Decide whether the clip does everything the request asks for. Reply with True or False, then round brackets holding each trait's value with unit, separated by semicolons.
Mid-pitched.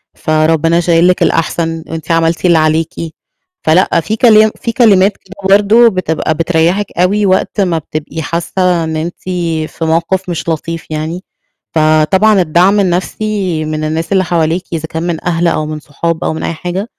True (170 Hz)